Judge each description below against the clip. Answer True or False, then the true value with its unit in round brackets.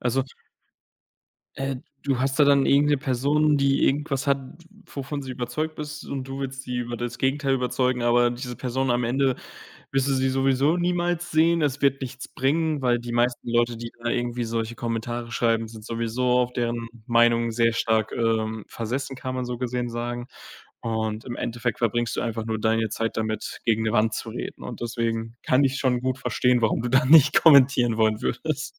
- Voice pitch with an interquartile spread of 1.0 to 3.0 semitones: True (2.6 semitones)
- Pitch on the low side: True (125 Hz)